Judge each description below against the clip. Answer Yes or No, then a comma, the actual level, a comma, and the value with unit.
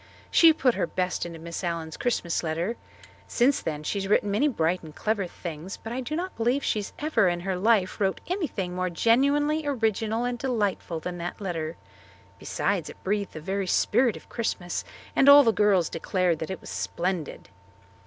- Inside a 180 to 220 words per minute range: Yes, average, 185 wpm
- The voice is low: No, high, 195 Hz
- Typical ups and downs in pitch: No, wide, 5.7 semitones